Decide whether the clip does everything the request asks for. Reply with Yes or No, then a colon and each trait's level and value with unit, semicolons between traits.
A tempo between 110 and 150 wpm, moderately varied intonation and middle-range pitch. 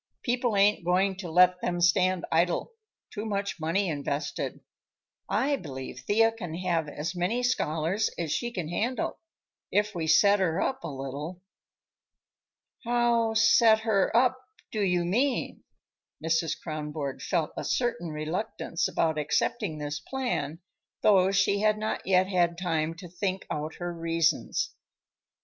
Yes: average, 140 wpm; average, 4.8 semitones; medium, 180 Hz